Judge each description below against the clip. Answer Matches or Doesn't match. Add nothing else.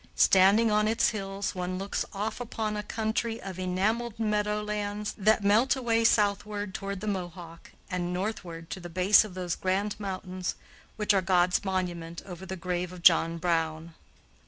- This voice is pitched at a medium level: Doesn't match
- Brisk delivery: Doesn't match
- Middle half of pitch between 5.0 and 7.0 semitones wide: Doesn't match